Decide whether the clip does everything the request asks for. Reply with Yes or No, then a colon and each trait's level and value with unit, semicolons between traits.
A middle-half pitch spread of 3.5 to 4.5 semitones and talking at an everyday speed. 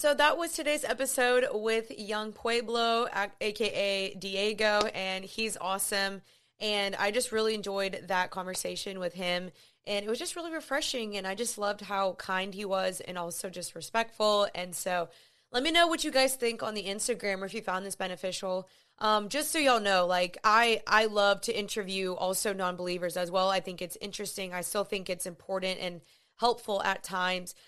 No: average, 3.1 semitones; average, 185 wpm